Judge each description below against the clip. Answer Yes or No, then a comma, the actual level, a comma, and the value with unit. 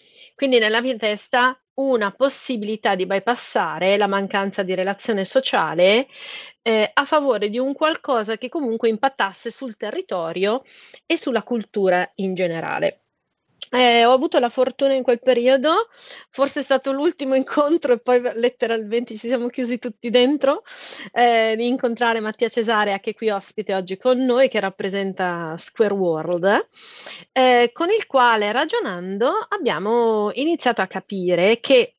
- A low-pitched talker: No, high, 240 Hz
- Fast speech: No, average, 145 wpm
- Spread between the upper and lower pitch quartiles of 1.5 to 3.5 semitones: No, average, 4.5 semitones